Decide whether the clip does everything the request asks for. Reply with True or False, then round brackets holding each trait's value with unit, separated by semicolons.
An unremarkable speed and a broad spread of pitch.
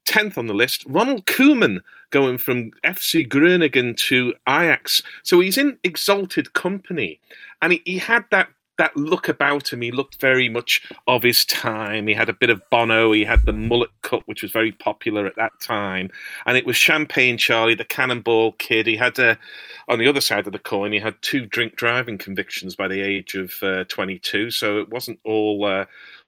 True (195 wpm; 6.1 semitones)